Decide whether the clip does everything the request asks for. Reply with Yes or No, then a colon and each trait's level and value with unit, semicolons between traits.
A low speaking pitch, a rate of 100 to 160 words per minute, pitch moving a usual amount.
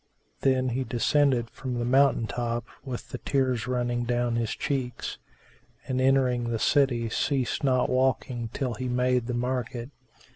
No: low, 125 Hz; average, 150 wpm; narrow, 1.6 semitones